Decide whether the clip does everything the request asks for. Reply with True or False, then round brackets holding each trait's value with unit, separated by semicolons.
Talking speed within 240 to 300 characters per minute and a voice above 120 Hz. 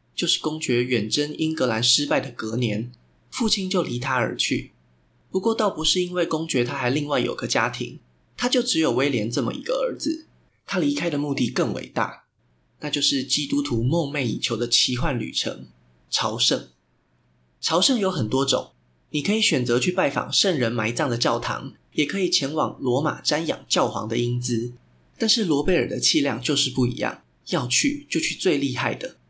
True (270 characters per minute; 140 Hz)